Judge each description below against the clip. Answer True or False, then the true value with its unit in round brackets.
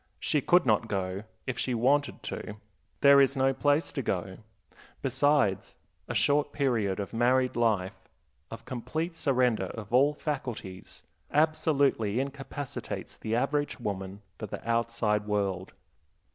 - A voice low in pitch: True (125 Hz)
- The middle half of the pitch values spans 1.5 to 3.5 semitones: False (5.2 semitones)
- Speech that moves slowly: True (130 wpm)